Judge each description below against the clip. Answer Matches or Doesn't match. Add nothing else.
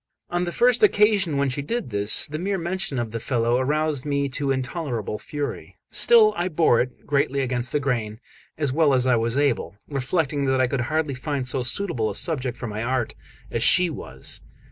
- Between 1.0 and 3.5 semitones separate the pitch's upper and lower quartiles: Doesn't match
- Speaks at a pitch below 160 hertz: Matches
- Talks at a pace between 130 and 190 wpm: Doesn't match